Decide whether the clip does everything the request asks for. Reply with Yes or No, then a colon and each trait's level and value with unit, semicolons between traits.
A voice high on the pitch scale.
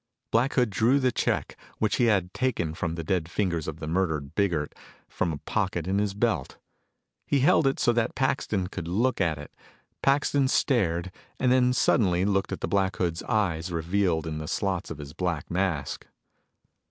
No: very low, 95 Hz